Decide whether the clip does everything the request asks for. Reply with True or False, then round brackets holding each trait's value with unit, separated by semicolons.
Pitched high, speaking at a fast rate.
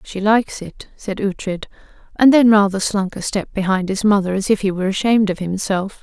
True (200 Hz; 210 wpm)